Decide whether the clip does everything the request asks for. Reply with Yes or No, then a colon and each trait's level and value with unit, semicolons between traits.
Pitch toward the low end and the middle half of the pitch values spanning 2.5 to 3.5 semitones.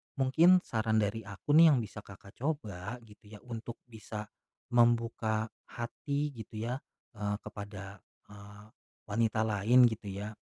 Yes: low, 110 Hz; average, 2.8 semitones